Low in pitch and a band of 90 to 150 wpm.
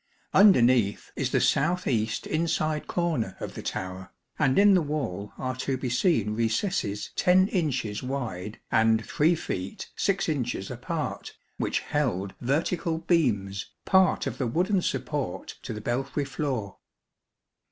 Yes: low, 130 Hz; average, 140 wpm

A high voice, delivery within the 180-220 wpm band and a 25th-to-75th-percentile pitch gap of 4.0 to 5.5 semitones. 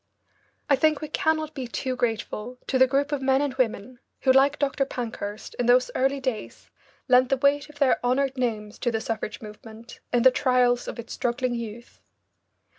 No: very high, 255 Hz; average, 190 wpm; narrow, 2.6 semitones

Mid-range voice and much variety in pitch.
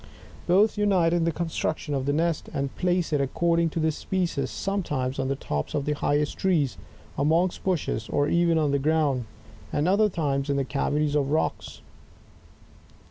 No: medium, 155 Hz; average, 3.5 semitones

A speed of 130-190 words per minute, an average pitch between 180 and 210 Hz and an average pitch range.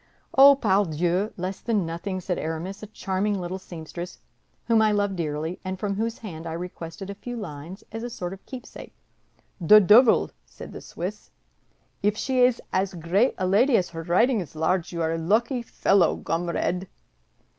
Yes: average, 175 wpm; high, 190 Hz; average, 3.9 semitones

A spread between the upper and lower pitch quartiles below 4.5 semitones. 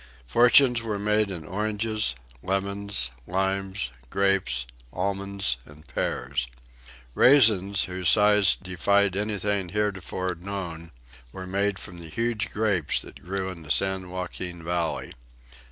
Yes: average, 2.7 semitones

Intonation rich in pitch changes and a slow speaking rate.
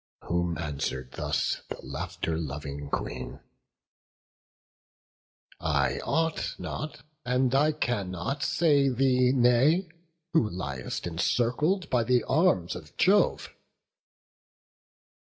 Yes: wide, 8.9 semitones; slow, 95 wpm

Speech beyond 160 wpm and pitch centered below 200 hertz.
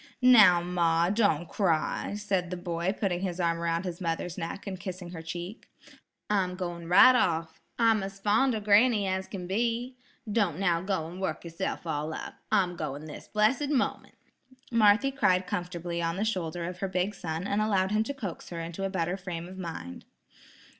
Yes: average, 190 wpm; medium, 185 Hz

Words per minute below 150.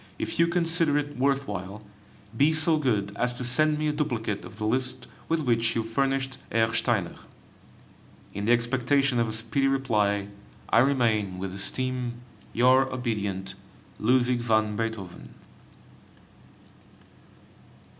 Yes: slow, 135 wpm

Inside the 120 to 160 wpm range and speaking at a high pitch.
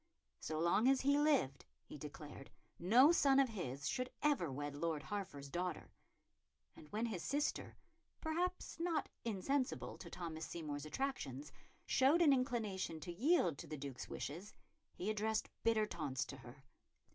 Yes: average, 150 wpm; high, 195 Hz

